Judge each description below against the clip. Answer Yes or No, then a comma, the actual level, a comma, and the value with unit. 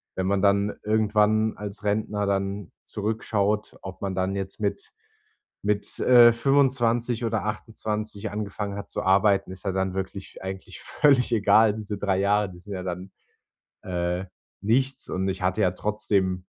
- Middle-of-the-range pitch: No, low, 100 Hz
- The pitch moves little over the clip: Yes, narrow, 2.2 semitones